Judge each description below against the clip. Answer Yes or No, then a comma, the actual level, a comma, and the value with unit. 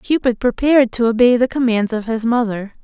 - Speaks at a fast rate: No, average, 190 wpm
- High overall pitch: Yes, high, 235 Hz